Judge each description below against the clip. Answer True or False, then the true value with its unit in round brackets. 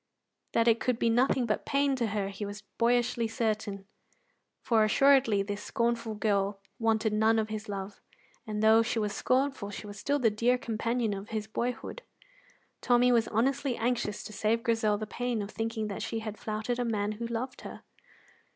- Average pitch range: False (2.2 semitones)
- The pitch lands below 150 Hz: False (225 Hz)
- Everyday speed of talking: True (185 wpm)